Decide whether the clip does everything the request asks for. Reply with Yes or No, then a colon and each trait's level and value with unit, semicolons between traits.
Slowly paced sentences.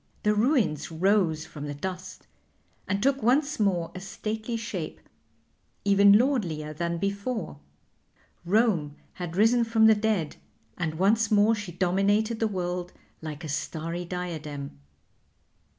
Yes: slow, 130 wpm